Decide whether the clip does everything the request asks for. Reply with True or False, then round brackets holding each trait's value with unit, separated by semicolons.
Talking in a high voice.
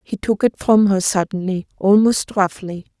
True (195 Hz)